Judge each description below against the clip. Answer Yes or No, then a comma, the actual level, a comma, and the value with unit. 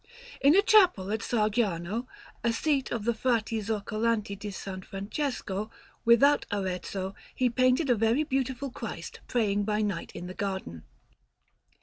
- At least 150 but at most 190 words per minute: No, average, 140 wpm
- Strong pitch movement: No, average, 4.1 semitones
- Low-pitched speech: No, high, 220 Hz